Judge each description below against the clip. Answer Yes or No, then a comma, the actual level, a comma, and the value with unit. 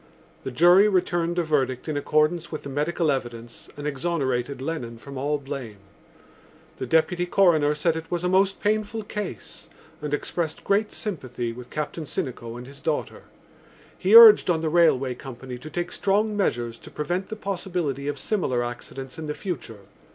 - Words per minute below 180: Yes, average, 170 wpm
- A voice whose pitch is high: No, medium, 150 Hz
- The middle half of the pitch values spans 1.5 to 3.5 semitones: No, average, 5.1 semitones